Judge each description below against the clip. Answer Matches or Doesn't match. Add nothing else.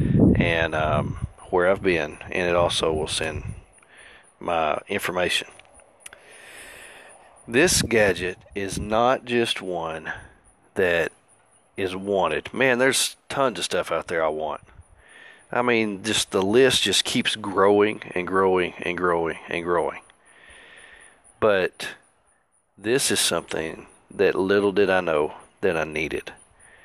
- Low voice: Matches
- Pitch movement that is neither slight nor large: Matches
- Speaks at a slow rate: Matches